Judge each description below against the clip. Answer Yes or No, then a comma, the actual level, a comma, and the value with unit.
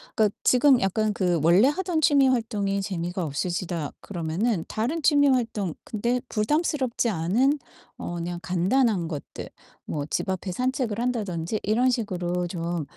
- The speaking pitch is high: Yes, high, 205 Hz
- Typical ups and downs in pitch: No, wide, 6.2 semitones